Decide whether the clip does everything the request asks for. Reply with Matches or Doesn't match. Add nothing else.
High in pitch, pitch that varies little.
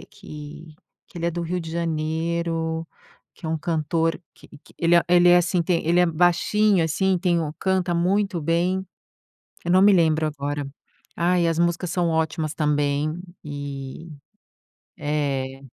Doesn't match